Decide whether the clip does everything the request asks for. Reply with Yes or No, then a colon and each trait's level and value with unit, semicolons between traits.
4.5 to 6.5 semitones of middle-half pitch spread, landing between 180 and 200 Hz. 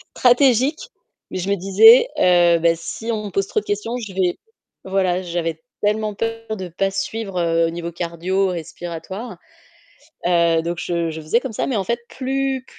Yes: average, 4.8 semitones; high, 190 Hz